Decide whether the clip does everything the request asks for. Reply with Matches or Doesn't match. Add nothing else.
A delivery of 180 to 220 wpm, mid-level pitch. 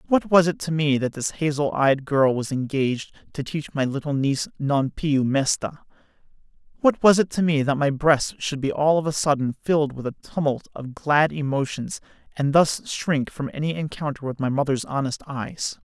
Matches